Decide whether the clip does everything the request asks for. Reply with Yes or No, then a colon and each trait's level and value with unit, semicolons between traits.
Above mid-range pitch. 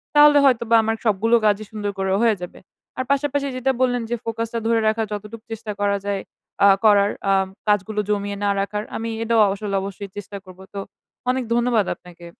Yes: high, 215 Hz